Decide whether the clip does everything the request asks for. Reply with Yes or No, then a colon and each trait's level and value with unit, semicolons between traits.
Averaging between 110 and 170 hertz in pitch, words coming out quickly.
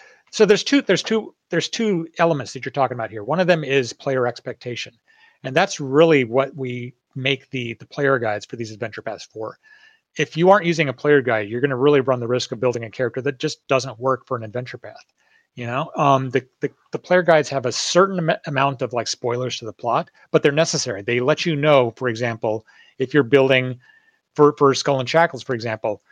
Yes: low, 135 Hz; fast, 225 wpm